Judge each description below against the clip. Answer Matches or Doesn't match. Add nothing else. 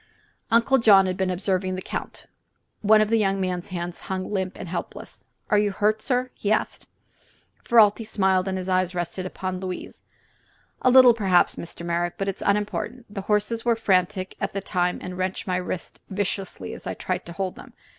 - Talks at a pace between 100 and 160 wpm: Doesn't match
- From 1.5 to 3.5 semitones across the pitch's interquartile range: Matches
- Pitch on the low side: Doesn't match